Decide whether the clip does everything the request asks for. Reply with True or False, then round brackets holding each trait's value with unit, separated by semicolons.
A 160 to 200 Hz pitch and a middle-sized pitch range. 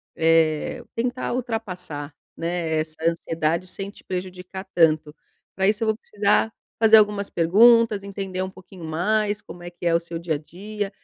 True (185 Hz; 4.1 semitones)